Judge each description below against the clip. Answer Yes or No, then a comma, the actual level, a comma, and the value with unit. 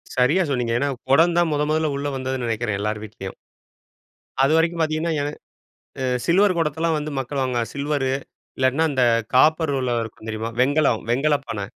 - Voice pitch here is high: No, medium, 140 Hz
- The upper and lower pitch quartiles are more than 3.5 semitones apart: Yes, average, 4.3 semitones